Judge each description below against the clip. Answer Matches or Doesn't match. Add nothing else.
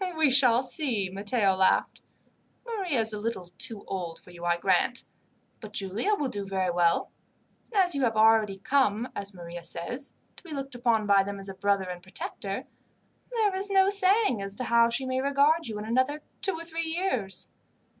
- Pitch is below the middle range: Doesn't match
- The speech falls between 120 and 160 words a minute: Doesn't match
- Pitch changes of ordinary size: Doesn't match